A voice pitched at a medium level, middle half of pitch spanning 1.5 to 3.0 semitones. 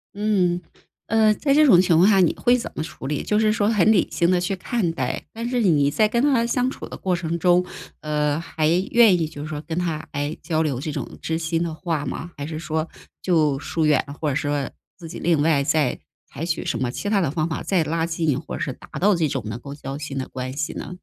No: medium, 165 Hz; average, 4.1 semitones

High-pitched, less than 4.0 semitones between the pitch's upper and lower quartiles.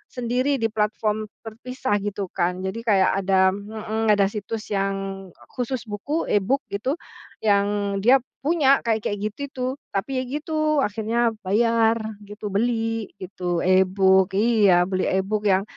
Yes: high, 210 Hz; average, 3.2 semitones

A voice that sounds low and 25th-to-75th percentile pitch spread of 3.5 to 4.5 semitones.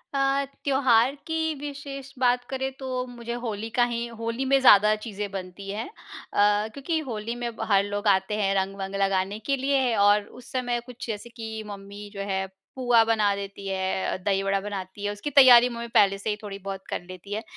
No: high, 215 Hz; average, 3.9 semitones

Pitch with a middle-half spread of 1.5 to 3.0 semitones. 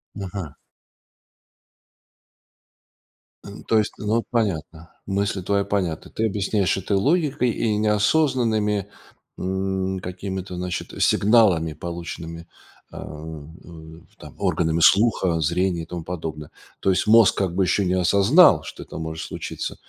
No: average, 3.4 semitones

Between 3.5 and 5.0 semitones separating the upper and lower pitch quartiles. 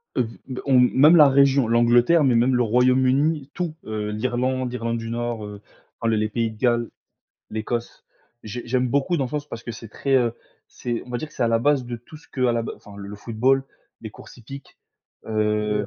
No: average, 2.7 semitones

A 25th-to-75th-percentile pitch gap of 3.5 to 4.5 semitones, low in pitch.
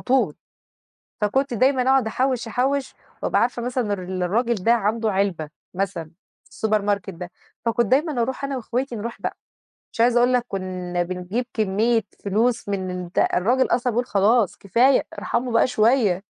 No: average, 4.2 semitones; high, 225 Hz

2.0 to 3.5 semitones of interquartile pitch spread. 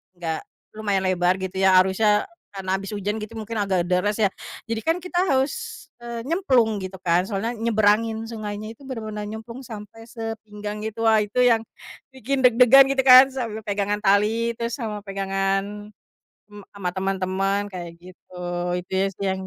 Yes: average, 2.8 semitones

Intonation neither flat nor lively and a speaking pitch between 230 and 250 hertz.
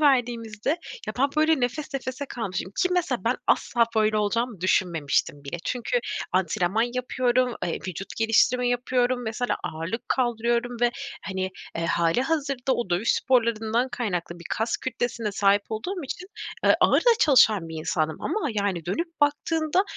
Yes: average, 4.8 semitones; high, 235 Hz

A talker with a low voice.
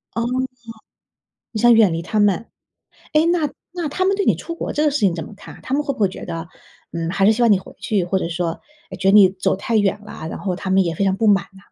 No: high, 200 Hz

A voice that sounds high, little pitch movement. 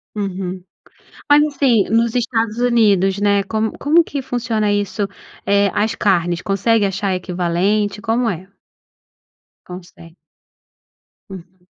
No: high, 205 Hz; average, 3.3 semitones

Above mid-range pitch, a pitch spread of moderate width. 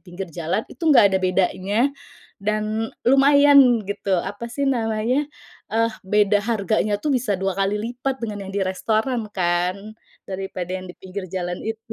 Yes: high, 210 Hz; average, 3.5 semitones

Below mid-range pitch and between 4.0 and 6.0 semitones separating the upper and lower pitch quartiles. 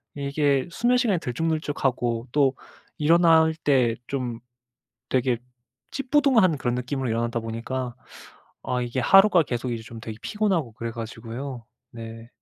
Yes: low, 130 Hz; wide, 5.4 semitones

